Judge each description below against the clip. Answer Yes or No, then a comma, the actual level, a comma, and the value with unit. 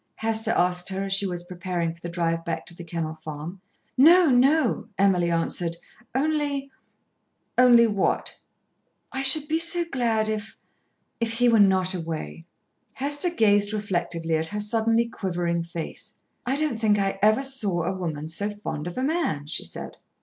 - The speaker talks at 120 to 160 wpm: No, average, 170 wpm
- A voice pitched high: Yes, high, 200 Hz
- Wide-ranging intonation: Yes, wide, 6.1 semitones